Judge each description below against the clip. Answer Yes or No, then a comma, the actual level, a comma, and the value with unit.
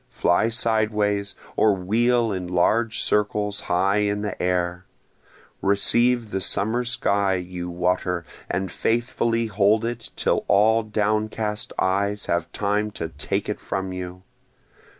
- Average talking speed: No, slow, 130 wpm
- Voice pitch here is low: Yes, low, 105 Hz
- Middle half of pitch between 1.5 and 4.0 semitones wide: Yes, average, 3.1 semitones